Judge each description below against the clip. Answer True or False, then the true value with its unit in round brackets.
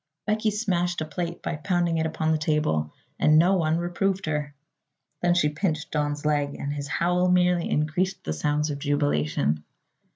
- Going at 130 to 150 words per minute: False (170 wpm)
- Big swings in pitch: False (3.2 semitones)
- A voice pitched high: False (155 Hz)